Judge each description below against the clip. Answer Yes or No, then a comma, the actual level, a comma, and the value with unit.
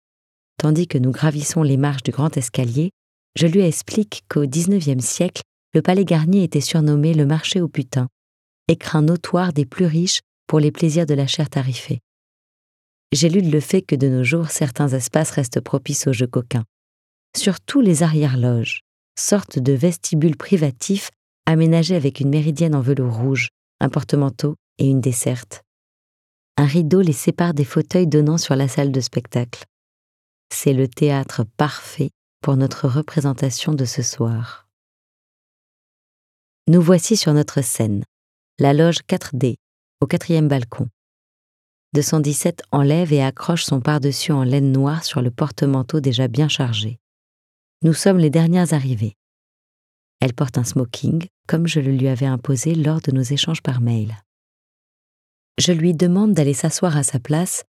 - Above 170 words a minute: No, average, 155 wpm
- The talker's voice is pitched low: No, medium, 145 Hz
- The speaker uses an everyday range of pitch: Yes, average, 3.9 semitones